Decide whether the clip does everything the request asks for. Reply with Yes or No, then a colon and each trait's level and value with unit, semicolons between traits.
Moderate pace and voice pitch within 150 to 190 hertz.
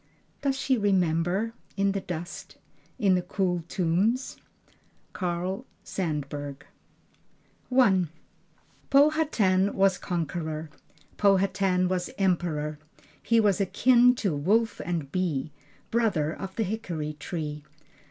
No: slow, 105 wpm; medium, 185 Hz